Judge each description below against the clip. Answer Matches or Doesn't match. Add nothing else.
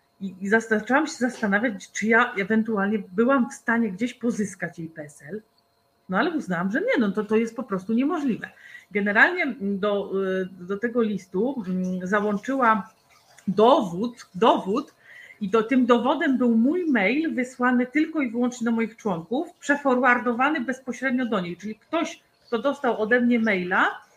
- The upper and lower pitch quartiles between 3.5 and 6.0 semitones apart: Matches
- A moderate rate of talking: Matches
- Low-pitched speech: Doesn't match